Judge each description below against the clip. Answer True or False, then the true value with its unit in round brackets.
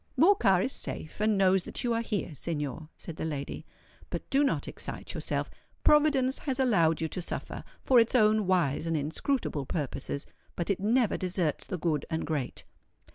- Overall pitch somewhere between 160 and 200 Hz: True (185 Hz)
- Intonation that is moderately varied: False (7.1 semitones)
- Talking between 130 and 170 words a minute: False (180 wpm)